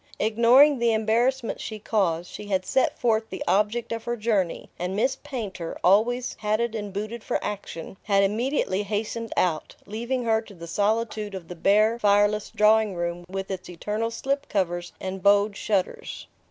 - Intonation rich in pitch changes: No, average, 3.0 semitones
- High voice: Yes, high, 210 Hz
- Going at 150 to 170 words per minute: Yes, average, 165 wpm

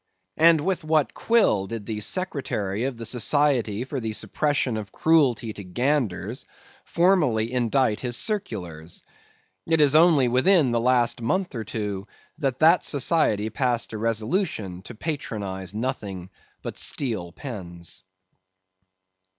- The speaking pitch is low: Yes, low, 120 Hz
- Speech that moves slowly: Yes, slow, 130 wpm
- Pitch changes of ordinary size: No, wide, 5.9 semitones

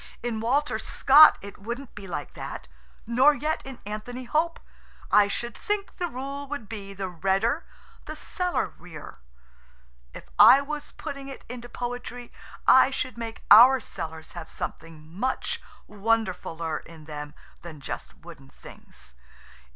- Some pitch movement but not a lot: No, wide, 7.3 semitones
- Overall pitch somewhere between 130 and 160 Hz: No, high, 230 Hz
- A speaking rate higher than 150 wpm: No, average, 140 wpm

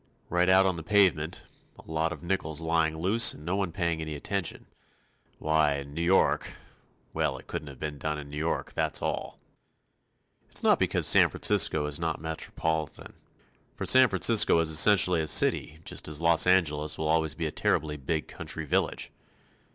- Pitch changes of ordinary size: No, narrow, 2.3 semitones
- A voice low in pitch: Yes, very low, 80 Hz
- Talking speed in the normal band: Yes, average, 175 wpm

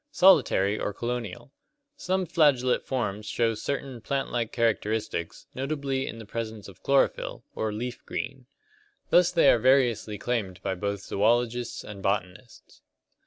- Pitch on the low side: Yes, low, 115 Hz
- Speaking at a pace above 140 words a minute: No, slow, 135 wpm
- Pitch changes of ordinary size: Yes, average, 4.1 semitones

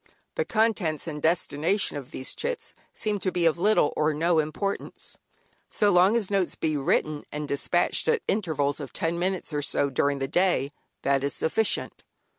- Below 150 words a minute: No, average, 175 wpm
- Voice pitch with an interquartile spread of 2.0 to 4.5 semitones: No, average, 5.2 semitones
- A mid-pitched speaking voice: Yes, medium, 165 Hz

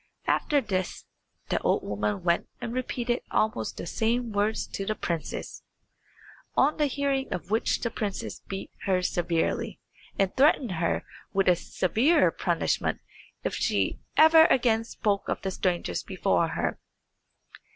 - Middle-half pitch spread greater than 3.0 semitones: Yes, wide, 5.4 semitones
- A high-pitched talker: Yes, high, 215 Hz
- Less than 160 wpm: Yes, average, 140 wpm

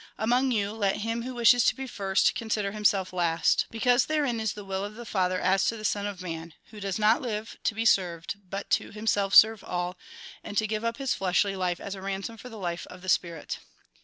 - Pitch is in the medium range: No, high, 205 Hz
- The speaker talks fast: Yes, fast, 235 wpm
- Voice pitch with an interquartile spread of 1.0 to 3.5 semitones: Yes, average, 3.0 semitones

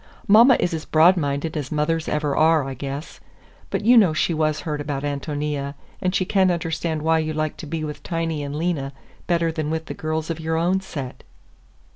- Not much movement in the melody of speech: Yes, narrow, 2.1 semitones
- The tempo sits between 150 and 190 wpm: No, fast, 205 wpm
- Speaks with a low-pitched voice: No, medium, 155 Hz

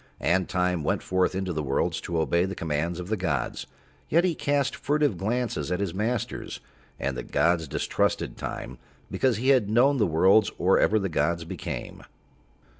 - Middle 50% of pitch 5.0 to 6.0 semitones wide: Yes, wide, 5.5 semitones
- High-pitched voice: No, very low, 95 Hz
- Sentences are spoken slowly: No, average, 180 wpm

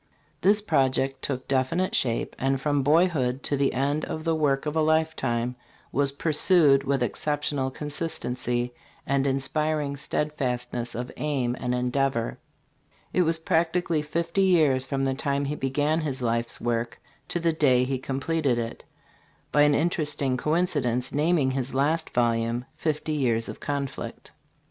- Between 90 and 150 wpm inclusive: Yes, average, 145 wpm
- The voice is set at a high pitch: No, medium, 140 Hz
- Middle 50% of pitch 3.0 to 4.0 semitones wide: Yes, average, 3.4 semitones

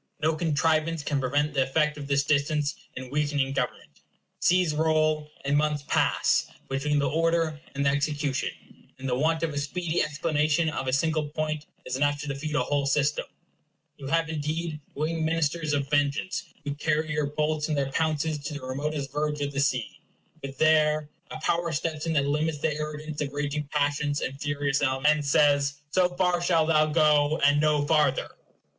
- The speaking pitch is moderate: Yes, medium, 150 Hz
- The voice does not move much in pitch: Yes, narrow, 1.5 semitones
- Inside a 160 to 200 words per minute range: Yes, average, 185 wpm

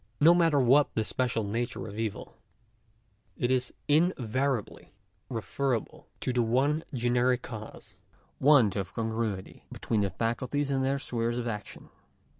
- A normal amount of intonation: Yes, average, 3.4 semitones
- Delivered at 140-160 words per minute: Yes, average, 145 wpm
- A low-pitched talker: Yes, low, 120 Hz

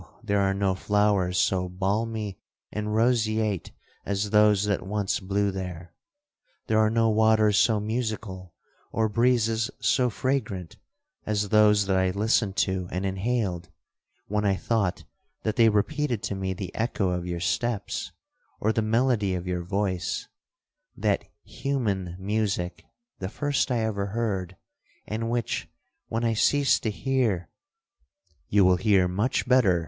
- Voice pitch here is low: Yes, low, 105 Hz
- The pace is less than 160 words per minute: Yes, average, 140 wpm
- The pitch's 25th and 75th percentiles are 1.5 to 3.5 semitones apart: Yes, average, 3.0 semitones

